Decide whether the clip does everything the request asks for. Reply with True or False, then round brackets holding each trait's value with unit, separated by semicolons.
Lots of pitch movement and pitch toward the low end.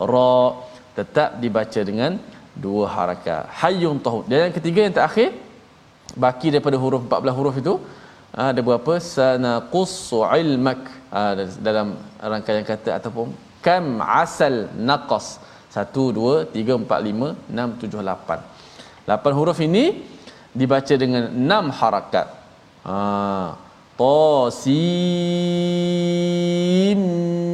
True (7.4 semitones; 130 Hz)